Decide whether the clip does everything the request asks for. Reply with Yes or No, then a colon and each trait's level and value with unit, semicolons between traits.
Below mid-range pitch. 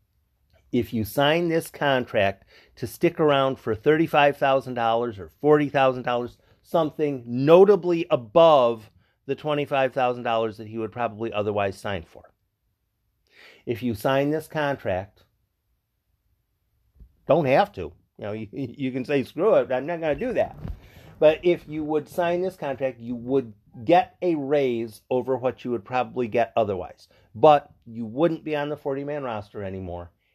Yes: low, 125 Hz